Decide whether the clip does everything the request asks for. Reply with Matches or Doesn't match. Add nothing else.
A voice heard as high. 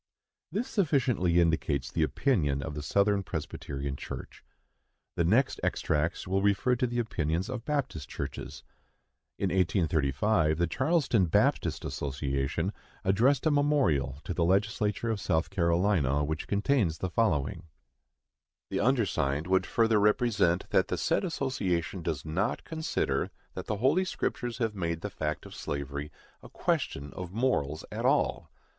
Doesn't match